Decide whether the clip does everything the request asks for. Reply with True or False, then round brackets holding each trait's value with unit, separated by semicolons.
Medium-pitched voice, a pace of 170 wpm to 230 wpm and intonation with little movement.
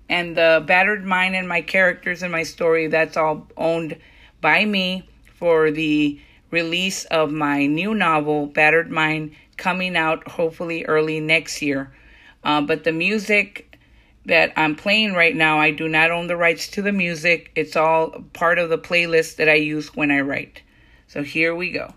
True (165 Hz; 175 wpm; 2.0 semitones)